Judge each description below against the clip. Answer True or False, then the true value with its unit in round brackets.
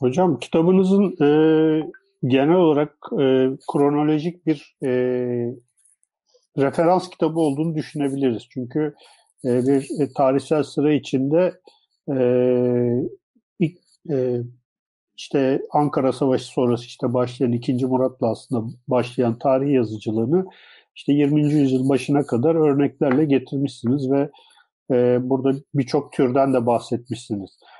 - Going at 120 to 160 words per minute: False (105 wpm)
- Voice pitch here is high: False (135 Hz)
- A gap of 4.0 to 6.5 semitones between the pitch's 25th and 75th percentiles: False (3.5 semitones)